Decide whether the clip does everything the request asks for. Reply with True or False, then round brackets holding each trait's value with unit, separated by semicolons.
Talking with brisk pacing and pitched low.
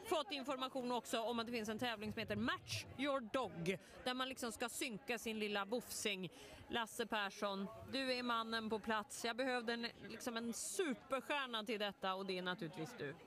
False (200 wpm; 230 Hz)